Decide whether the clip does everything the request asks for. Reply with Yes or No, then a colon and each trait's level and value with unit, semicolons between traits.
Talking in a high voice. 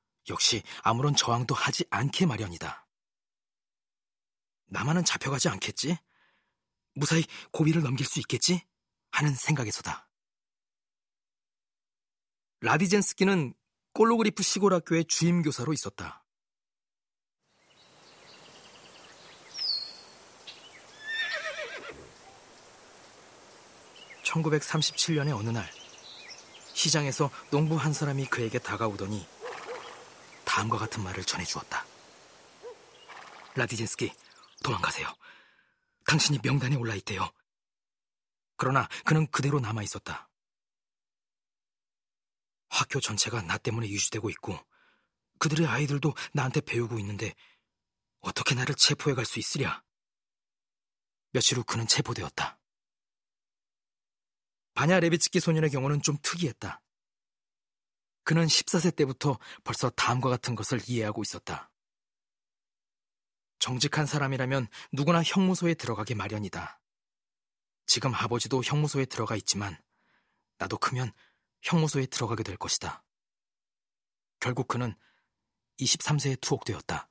No: medium, 140 Hz